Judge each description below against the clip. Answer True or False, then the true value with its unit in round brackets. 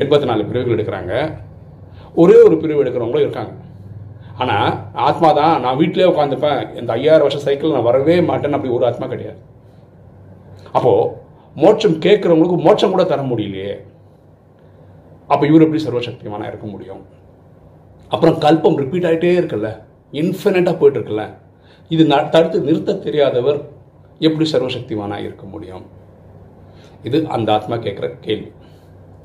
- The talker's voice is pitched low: True (125 Hz)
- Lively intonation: True (8.4 semitones)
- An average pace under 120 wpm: False (125 wpm)